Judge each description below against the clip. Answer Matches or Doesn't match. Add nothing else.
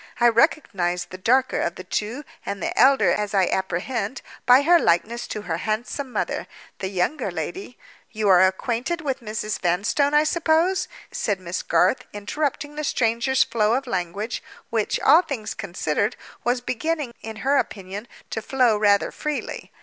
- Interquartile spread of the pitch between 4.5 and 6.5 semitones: Matches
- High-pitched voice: Matches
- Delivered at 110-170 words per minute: Matches